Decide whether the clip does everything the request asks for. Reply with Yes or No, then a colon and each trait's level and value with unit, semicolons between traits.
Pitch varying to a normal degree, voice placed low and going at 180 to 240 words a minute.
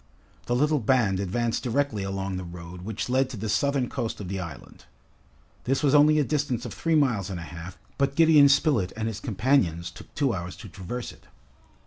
No: wide, 6.7 semitones; low, 115 Hz; average, 200 wpm